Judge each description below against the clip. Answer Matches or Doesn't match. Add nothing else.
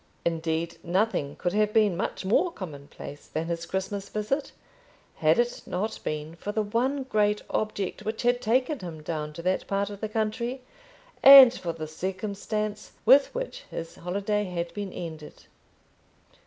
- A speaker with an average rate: Matches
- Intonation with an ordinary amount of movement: Matches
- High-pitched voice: Matches